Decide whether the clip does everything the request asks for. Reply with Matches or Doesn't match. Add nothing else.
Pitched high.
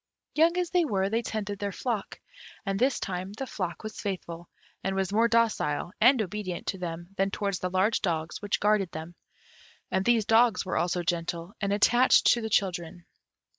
Matches